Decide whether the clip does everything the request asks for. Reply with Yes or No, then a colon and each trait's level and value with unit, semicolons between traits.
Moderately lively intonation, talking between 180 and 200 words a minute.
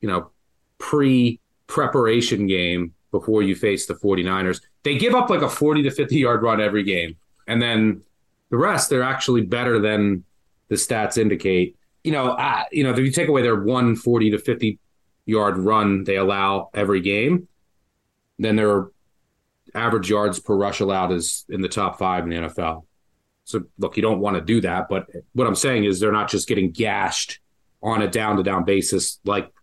Yes: average, 3.6 semitones; average, 185 wpm